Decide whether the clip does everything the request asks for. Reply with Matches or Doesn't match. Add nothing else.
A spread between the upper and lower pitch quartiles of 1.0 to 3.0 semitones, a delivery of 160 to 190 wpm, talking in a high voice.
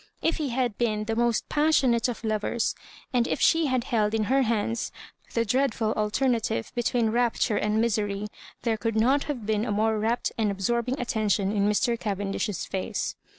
Matches